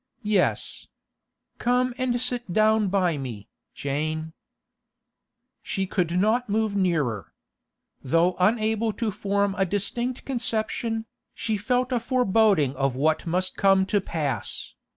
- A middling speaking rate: No, slow, 120 wpm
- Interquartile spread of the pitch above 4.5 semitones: Yes, average, 5.2 semitones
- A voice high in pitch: Yes, high, 200 Hz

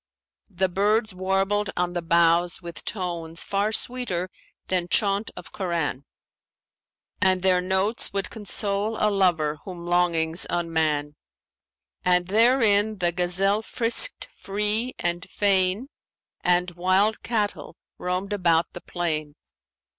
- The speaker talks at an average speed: No, slow, 115 wpm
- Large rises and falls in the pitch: No, average, 3.0 semitones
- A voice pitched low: No, medium, 185 Hz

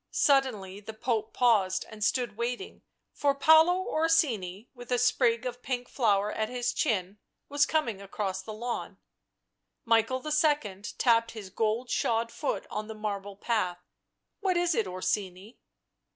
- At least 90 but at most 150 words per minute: Yes, average, 145 wpm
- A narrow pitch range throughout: No, average, 3.9 semitones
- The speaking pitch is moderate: No, high, 230 Hz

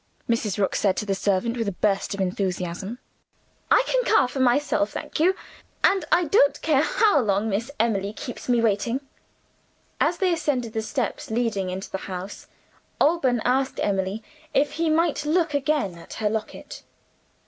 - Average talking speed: Yes, average, 170 wpm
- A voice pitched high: Yes, high, 230 Hz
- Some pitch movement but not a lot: No, wide, 6.6 semitones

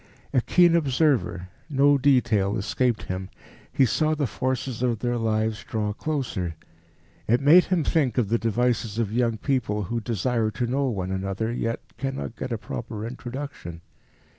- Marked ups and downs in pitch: No, average, 3.7 semitones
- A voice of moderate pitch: No, low, 120 Hz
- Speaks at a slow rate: No, average, 160 wpm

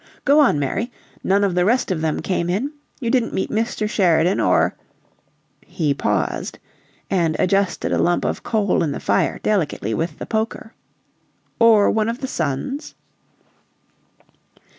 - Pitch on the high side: Yes, high, 195 Hz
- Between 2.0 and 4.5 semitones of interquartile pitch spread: No, average, 5.1 semitones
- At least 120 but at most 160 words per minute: Yes, average, 155 wpm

